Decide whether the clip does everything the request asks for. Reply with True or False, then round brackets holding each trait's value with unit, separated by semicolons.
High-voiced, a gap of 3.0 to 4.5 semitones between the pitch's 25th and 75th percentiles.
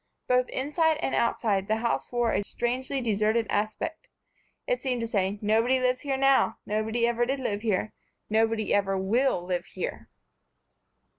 True (230 Hz; 3.4 semitones)